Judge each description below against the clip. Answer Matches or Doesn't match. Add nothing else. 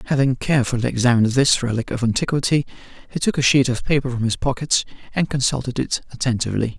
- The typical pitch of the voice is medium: Doesn't match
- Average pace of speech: Matches